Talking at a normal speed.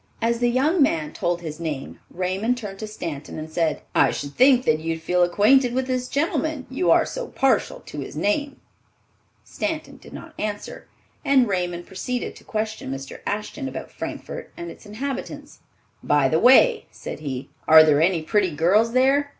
Yes: average, 175 wpm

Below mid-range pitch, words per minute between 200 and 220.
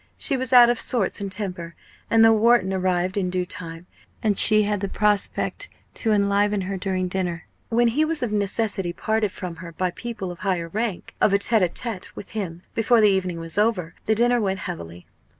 No: high, 200 Hz; fast, 205 wpm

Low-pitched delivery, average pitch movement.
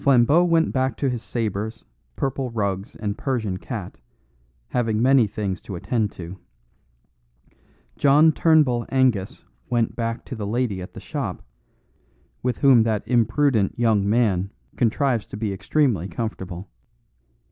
Yes: low, 115 Hz; average, 4.3 semitones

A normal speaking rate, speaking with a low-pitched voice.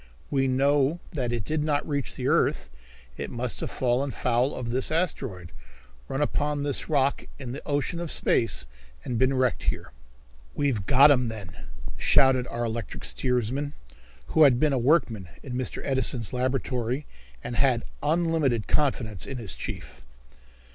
Yes: average, 155 wpm; low, 130 Hz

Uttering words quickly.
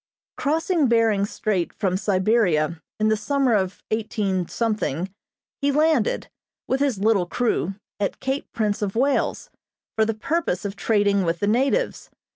No: average, 140 wpm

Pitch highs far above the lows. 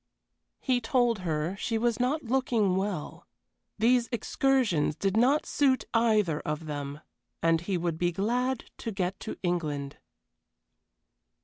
Yes: wide, 6.7 semitones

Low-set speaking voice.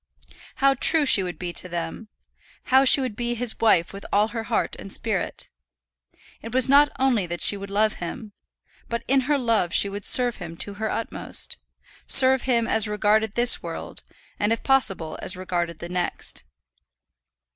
No: high, 220 Hz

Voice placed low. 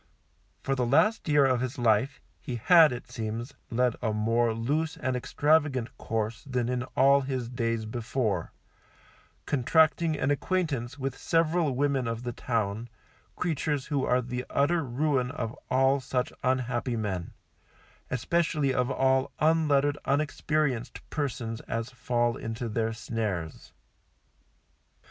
Yes: low, 125 Hz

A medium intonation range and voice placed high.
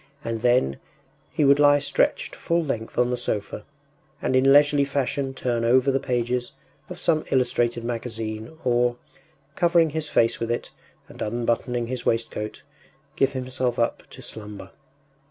No: average, 3.0 semitones; low, 125 Hz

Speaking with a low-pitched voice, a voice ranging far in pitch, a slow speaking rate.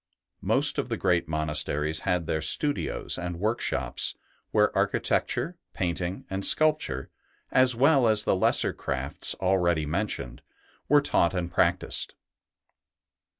Yes: very low, 90 Hz; wide, 6.1 semitones; slow, 125 wpm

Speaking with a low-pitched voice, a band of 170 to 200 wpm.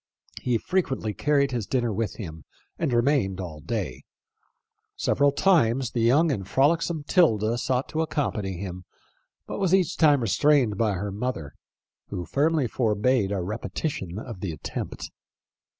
No: low, 120 Hz; average, 145 wpm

